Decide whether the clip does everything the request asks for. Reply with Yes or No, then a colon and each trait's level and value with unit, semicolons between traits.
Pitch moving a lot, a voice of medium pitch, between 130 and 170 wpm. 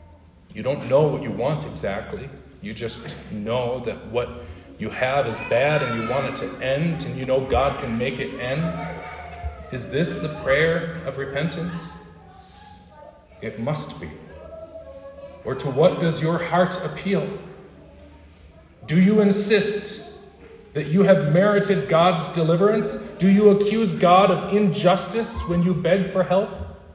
Yes: wide, 6.9 semitones; medium, 170 Hz; average, 145 wpm